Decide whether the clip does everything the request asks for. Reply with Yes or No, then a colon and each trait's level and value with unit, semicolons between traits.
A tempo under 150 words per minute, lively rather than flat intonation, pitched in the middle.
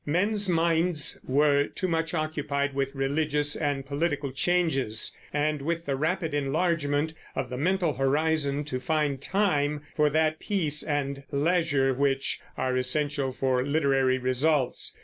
No: slow, 135 wpm; average, 2.7 semitones; medium, 145 Hz